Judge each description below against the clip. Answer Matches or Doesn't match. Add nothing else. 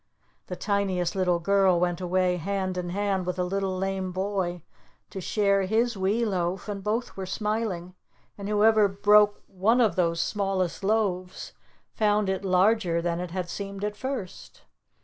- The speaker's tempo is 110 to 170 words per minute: Matches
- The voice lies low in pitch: Doesn't match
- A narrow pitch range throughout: Matches